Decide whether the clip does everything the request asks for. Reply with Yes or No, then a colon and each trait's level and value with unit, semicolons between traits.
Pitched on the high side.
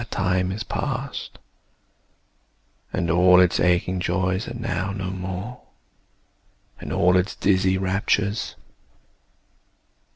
No: very low, 95 Hz